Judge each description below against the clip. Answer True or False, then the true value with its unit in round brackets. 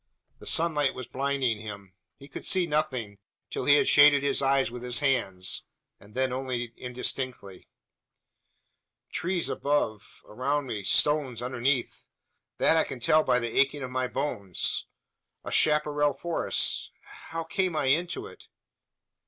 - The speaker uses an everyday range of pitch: True (3.3 semitones)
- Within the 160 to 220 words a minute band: False (140 wpm)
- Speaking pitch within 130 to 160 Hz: True (135 Hz)